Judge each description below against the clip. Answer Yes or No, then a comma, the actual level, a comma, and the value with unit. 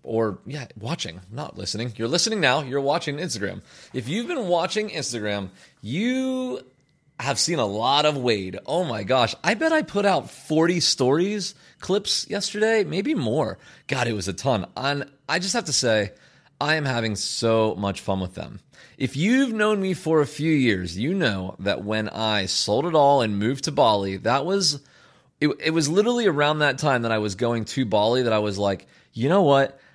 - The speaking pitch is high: No, medium, 140 Hz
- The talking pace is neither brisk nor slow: Yes, average, 195 wpm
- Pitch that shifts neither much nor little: No, wide, 8.3 semitones